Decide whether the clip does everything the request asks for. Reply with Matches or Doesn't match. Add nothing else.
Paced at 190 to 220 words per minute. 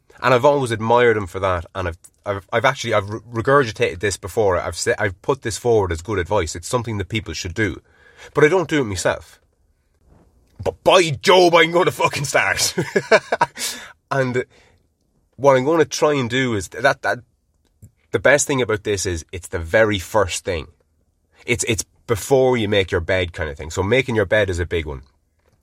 Matches